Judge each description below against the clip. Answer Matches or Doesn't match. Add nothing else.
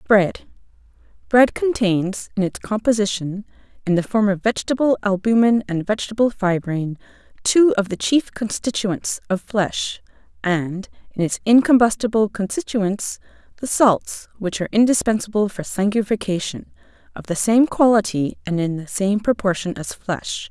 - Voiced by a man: Doesn't match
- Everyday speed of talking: Doesn't match